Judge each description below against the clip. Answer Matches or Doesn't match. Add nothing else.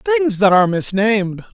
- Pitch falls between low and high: Doesn't match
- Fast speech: Doesn't match